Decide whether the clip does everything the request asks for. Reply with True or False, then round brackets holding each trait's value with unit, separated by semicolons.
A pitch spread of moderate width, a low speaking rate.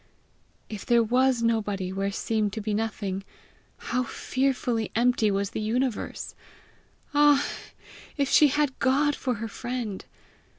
True (3.8 semitones; 130 wpm)